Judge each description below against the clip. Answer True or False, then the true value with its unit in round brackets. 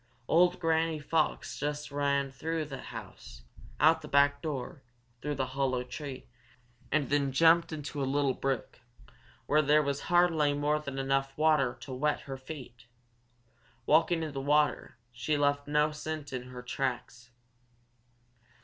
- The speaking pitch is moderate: True (145 Hz)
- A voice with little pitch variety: True (2.2 semitones)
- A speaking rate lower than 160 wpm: True (150 wpm)